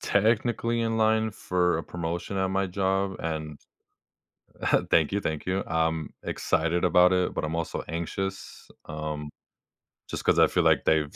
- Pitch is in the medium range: No, very low, 90 Hz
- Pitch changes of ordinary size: Yes, average, 3.4 semitones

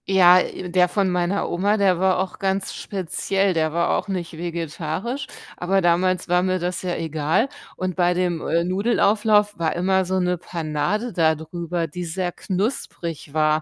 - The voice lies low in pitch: No, medium, 180 Hz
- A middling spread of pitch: No, narrow, 2.2 semitones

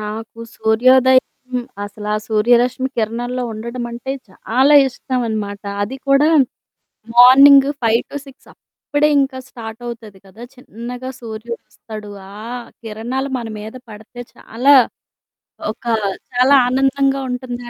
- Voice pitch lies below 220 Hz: No, high, 245 Hz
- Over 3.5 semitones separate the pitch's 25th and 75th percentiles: No, average, 3.0 semitones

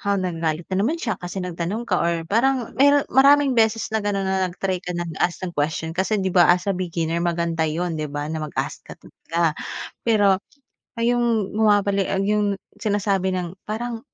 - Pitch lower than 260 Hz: Yes, high, 190 Hz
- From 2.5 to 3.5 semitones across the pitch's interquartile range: No, average, 4.1 semitones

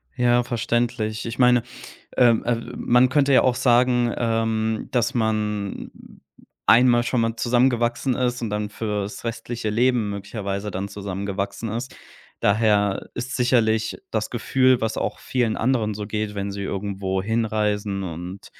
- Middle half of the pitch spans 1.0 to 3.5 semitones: Yes, average, 2.8 semitones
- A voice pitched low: Yes, low, 110 Hz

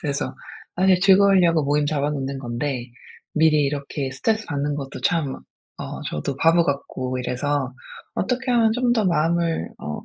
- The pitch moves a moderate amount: Yes, average, 4.6 semitones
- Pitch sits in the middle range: Yes, medium, 150 Hz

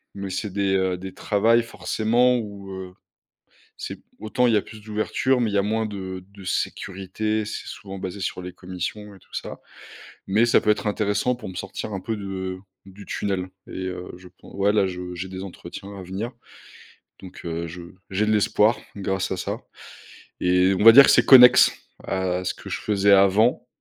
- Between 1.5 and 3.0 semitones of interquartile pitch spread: Yes, narrow, 2.4 semitones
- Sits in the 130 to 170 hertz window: No, low, 100 Hz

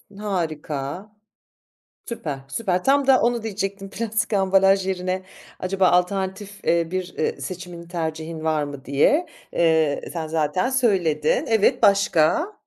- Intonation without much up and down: No, average, 4.3 semitones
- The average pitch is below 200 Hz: Yes, medium, 185 Hz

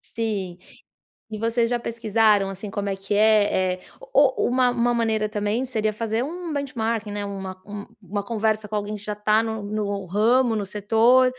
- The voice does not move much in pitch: Yes, narrow, 2.2 semitones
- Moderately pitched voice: No, high, 215 Hz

